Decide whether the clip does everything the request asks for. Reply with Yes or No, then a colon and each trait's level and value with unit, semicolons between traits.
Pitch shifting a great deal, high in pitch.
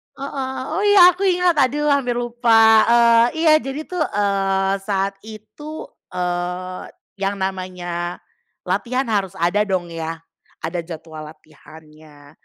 Yes: wide, 6.5 semitones; high, 200 Hz